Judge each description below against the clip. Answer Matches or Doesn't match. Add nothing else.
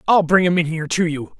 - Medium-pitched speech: Matches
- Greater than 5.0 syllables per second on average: Matches